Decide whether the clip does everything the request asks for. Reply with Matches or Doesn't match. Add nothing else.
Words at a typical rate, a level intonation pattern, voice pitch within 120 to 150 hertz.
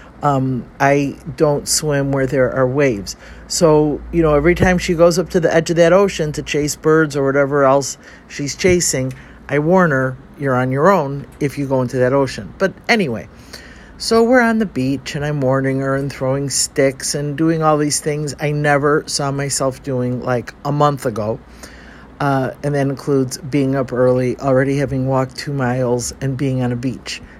Matches